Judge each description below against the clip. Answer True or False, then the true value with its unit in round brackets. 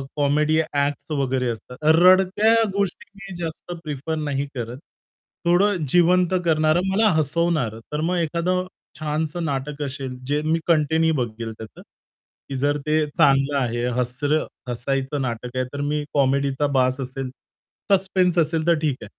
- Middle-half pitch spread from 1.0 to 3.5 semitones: False (4.0 semitones)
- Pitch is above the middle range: False (150 Hz)